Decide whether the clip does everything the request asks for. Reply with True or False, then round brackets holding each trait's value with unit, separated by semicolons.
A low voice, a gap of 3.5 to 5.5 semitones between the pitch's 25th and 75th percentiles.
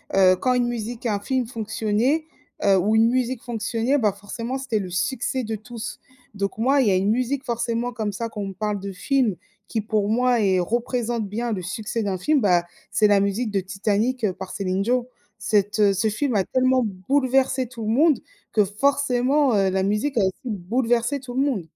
False (225 Hz; 3.9 semitones)